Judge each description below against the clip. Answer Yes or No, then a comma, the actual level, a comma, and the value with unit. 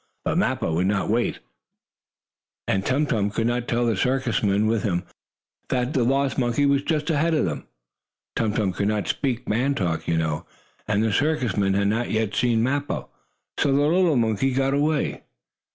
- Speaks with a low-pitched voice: Yes, low, 120 Hz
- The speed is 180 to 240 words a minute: Yes, average, 185 wpm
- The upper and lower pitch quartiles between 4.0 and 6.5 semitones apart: Yes, average, 5.1 semitones